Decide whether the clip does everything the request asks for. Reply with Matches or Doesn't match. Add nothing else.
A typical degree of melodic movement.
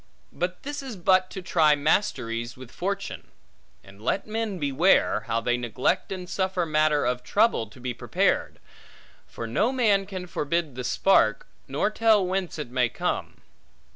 Doesn't match